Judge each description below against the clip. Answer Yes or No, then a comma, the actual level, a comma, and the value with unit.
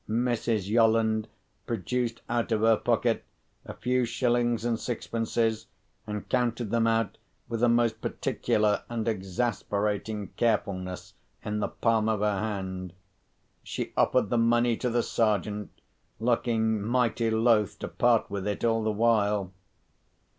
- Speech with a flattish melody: Yes, narrow, 2.0 semitones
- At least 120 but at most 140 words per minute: Yes, slow, 135 wpm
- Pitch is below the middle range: Yes, low, 115 Hz